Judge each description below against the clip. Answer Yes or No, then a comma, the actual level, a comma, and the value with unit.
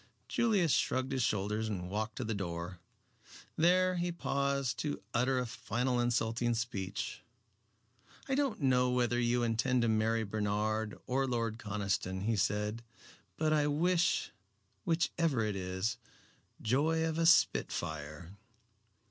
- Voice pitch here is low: Yes, low, 120 Hz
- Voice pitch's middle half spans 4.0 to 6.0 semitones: Yes, average, 4.9 semitones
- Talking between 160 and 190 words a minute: No, slow, 135 wpm